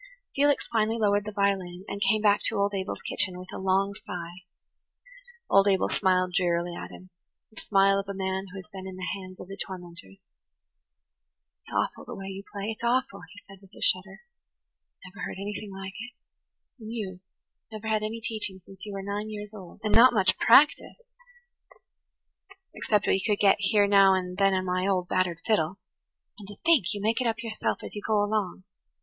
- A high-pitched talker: Yes, high, 195 Hz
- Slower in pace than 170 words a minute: No, average, 195 wpm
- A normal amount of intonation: No, narrow, 2.2 semitones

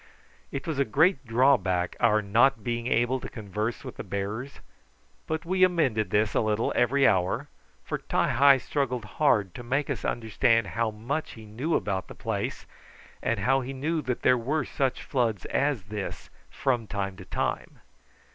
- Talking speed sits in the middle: Yes, average, 175 wpm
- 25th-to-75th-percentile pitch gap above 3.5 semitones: Yes, average, 4.4 semitones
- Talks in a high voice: No, low, 120 Hz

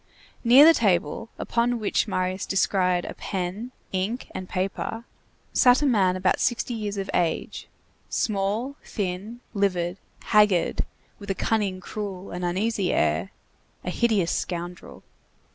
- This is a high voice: Yes, high, 195 Hz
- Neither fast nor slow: No, slow, 130 wpm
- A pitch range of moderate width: Yes, average, 3.7 semitones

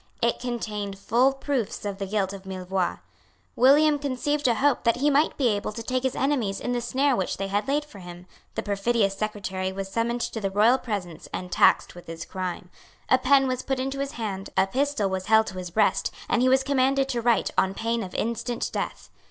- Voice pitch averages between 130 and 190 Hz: No, high, 230 Hz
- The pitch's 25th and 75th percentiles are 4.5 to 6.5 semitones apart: Yes, average, 5.1 semitones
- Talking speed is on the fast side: Yes, fast, 220 wpm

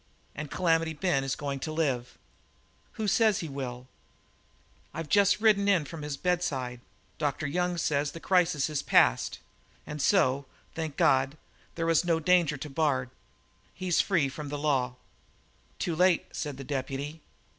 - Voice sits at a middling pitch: Yes, medium, 150 Hz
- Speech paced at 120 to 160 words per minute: Yes, average, 150 wpm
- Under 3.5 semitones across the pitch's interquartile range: No, average, 4.2 semitones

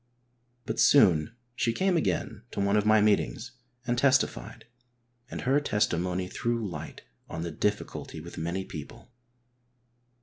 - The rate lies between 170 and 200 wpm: No, slow, 135 wpm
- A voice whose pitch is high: No, low, 105 Hz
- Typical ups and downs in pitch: No, wide, 5.7 semitones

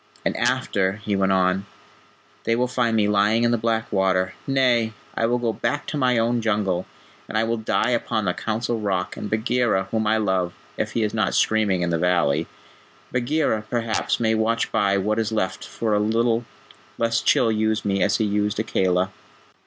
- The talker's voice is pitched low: Yes, low, 110 Hz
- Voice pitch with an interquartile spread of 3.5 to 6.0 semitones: No, average, 2.8 semitones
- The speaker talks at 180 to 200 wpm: Yes, average, 190 wpm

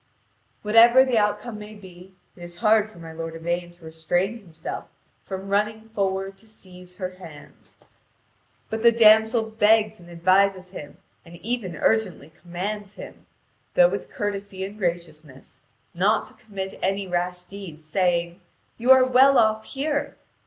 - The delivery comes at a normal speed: Yes, average, 150 wpm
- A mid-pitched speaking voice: No, high, 195 Hz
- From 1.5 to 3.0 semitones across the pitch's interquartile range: No, average, 3.8 semitones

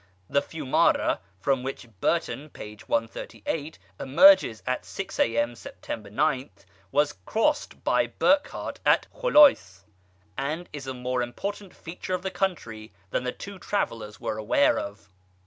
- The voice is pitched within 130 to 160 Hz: Yes, low, 135 Hz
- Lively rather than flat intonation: Yes, wide, 7.9 semitones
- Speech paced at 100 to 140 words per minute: Yes, slow, 135 wpm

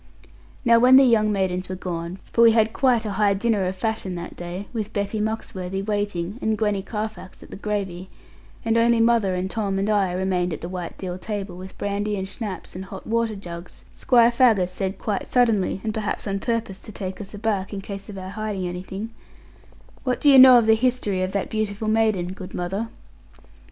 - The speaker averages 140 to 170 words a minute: No, fast, 205 wpm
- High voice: Yes, high, 205 Hz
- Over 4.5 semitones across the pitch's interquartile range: No, average, 2.9 semitones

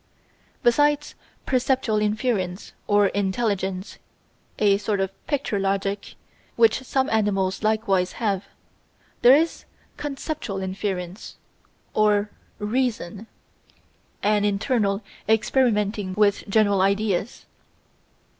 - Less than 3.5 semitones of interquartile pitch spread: Yes, average, 2.9 semitones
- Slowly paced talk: Yes, slow, 90 wpm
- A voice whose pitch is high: Yes, high, 210 Hz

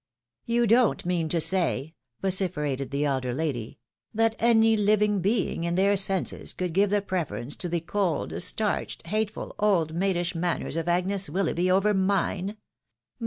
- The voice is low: No, medium, 185 Hz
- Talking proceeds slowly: No, average, 165 wpm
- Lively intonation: No, average, 3.7 semitones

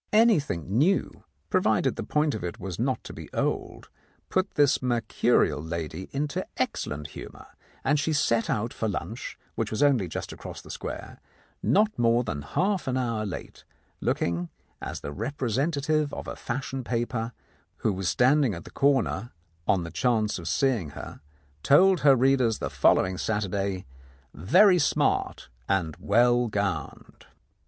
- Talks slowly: No, average, 150 wpm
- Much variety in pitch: Yes, wide, 6.8 semitones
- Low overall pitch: Yes, low, 120 Hz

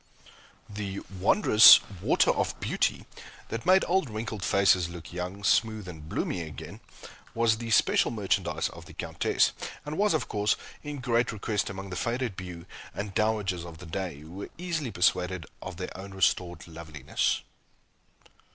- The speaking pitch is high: No, low, 100 Hz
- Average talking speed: Yes, average, 155 wpm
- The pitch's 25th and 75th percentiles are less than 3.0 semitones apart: No, average, 4.3 semitones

